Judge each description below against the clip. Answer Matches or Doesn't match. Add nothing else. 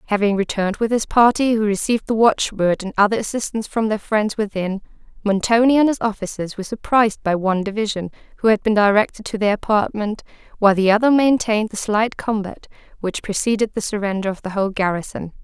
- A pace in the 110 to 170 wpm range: Doesn't match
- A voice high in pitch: Matches